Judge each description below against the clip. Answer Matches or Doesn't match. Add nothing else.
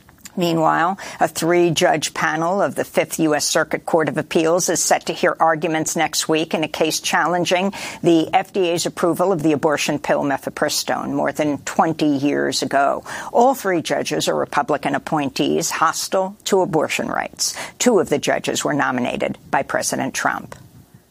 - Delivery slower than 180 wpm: Matches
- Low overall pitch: Doesn't match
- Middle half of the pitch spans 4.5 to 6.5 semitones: Doesn't match